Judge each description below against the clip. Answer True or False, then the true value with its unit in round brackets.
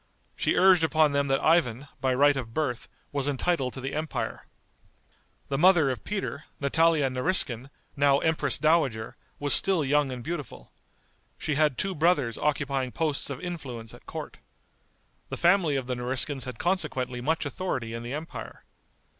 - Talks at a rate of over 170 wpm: False (160 wpm)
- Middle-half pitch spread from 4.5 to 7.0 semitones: False (3.9 semitones)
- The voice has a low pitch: False (145 Hz)